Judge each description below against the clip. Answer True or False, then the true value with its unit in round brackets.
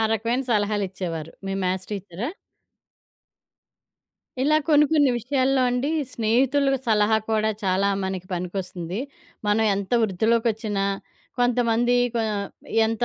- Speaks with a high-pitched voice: True (220 Hz)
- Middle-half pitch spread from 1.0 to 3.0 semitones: False (4.2 semitones)